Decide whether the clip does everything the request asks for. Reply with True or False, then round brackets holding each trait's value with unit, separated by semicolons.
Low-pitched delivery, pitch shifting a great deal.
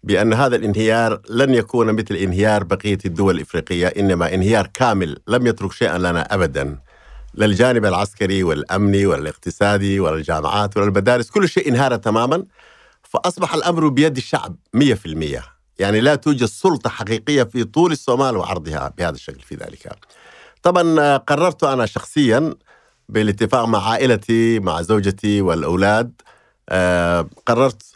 False (110 Hz; 4.3 semitones)